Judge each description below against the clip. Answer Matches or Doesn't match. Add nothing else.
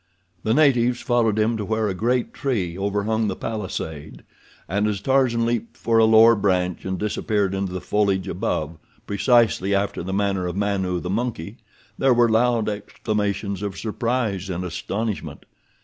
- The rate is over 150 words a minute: Matches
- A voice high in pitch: Doesn't match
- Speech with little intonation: Doesn't match